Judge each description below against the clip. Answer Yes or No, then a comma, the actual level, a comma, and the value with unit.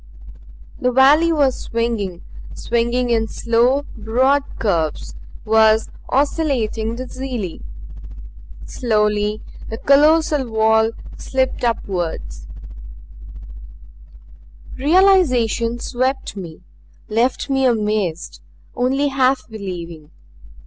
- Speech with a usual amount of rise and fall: Yes, average, 3.7 semitones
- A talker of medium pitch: No, high, 235 Hz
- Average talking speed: No, slow, 80 wpm